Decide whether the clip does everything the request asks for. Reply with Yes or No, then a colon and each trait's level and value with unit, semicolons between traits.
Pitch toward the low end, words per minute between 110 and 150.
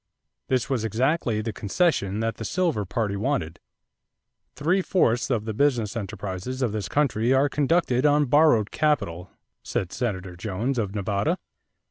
Yes: low, 115 Hz; average, 145 wpm